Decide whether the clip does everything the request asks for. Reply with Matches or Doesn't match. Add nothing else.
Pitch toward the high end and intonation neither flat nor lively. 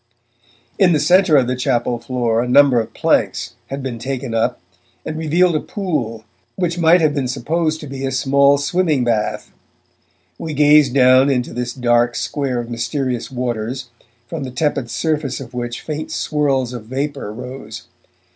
Doesn't match